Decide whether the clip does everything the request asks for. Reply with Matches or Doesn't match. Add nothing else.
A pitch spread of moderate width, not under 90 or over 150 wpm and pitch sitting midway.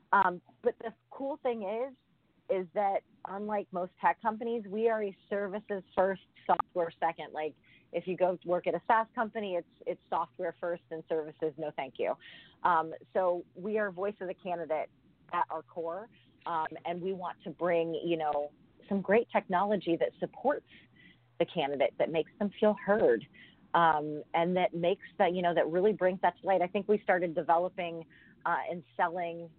Doesn't match